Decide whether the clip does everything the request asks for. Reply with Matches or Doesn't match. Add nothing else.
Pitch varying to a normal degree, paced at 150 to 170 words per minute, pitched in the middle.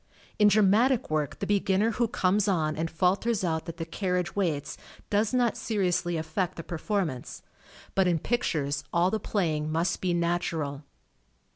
Matches